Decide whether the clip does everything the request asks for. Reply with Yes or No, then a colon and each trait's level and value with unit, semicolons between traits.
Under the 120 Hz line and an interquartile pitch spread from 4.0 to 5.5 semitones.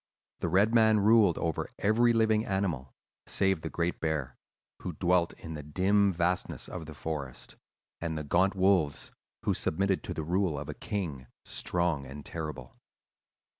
Yes: very low, 85 Hz; average, 4.4 semitones